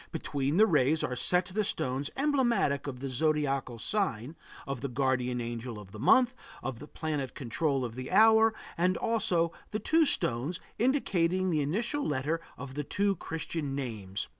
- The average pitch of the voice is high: No, medium, 145 Hz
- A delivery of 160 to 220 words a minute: Yes, average, 165 wpm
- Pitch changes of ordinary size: No, wide, 6.5 semitones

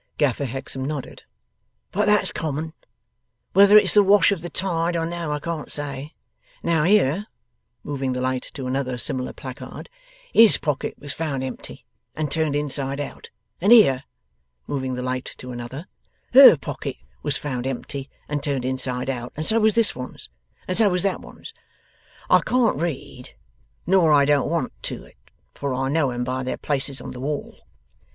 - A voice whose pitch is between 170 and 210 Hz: No, medium, 145 Hz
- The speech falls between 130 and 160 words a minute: No, average, 175 wpm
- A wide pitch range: No, average, 4.5 semitones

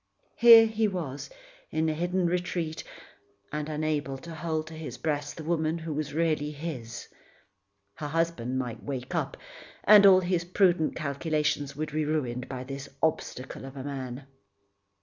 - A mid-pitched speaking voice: Yes, medium, 155 Hz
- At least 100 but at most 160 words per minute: Yes, average, 155 wpm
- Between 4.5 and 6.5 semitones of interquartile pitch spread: No, average, 3.3 semitones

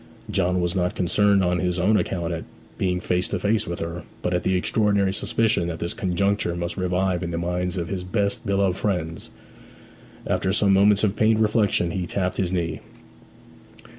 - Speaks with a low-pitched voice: Yes, very low, 90 Hz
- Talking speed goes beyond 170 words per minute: Yes, average, 185 wpm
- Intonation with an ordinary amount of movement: No, narrow, 2.3 semitones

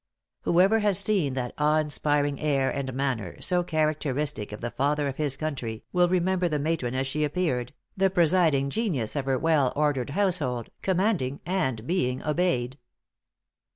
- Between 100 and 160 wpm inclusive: Yes, average, 155 wpm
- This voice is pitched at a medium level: Yes, medium, 150 Hz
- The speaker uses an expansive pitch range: No, average, 5.0 semitones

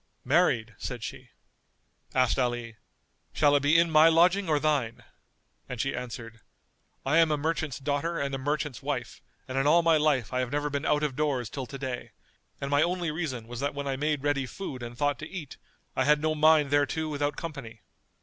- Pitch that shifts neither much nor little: Yes, average, 3.1 semitones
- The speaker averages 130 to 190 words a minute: No, fast, 205 wpm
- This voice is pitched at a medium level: Yes, medium, 145 Hz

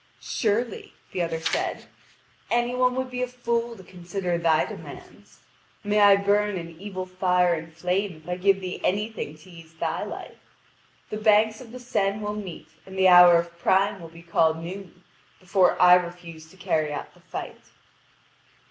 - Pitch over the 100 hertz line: Yes, medium, 185 Hz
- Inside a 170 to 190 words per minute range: Yes, average, 175 wpm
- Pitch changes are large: No, average, 3.5 semitones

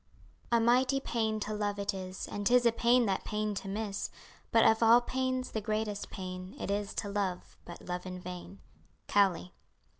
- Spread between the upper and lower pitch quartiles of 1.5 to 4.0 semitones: Yes, average, 3.1 semitones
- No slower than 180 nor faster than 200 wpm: Yes, average, 185 wpm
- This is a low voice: No, high, 205 Hz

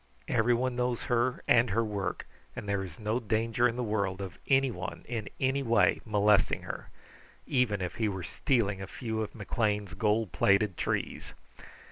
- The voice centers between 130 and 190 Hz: No, low, 110 Hz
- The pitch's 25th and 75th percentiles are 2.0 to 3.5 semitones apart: Yes, average, 3.2 semitones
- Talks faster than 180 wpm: No, average, 165 wpm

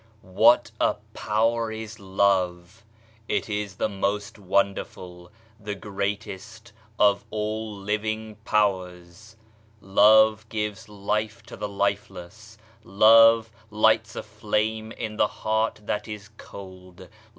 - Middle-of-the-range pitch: No, low, 105 Hz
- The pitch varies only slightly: Yes, narrow, 1.8 semitones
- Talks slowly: Yes, slow, 110 wpm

